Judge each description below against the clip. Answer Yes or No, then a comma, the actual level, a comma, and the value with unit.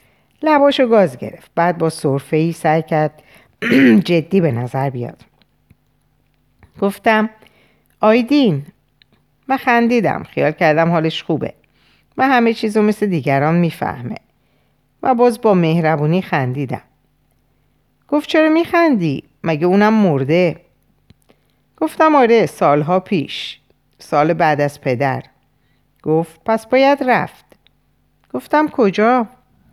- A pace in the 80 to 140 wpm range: Yes, slow, 105 wpm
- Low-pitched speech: No, medium, 185 Hz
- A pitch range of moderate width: No, wide, 7.6 semitones